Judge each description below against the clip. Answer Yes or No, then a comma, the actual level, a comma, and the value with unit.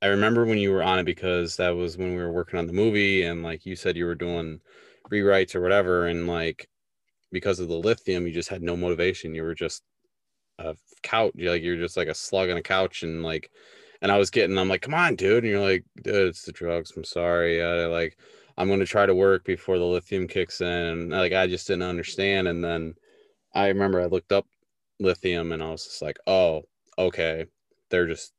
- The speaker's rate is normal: No, fast, 230 wpm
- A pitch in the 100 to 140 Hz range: No, very low, 90 Hz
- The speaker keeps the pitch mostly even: Yes, narrow, 2.0 semitones